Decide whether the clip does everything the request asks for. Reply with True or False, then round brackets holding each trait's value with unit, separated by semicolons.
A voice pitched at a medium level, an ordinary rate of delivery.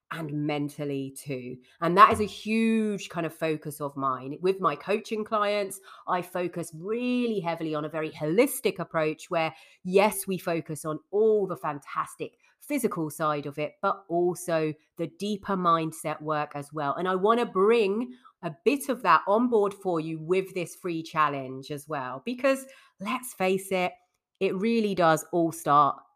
True (175 Hz; 165 wpm)